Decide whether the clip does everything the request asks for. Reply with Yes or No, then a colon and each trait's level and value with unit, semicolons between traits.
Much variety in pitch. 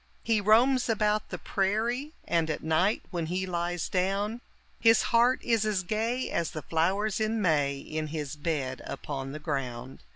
Yes: wide, 5.8 semitones